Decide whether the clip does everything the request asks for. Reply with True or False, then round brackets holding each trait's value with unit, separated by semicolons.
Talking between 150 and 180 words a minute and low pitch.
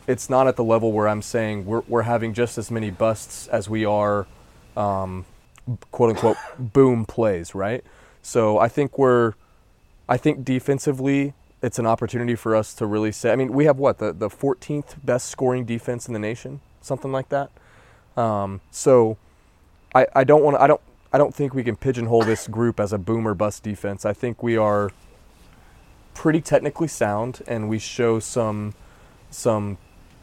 True (175 wpm; 115 Hz)